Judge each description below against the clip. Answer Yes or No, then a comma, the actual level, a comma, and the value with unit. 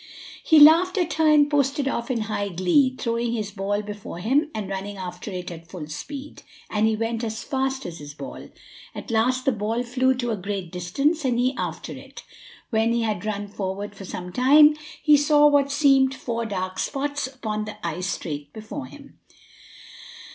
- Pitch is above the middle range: Yes, high, 230 Hz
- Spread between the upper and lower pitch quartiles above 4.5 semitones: Yes, wide, 5.4 semitones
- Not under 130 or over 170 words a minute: No, average, 190 wpm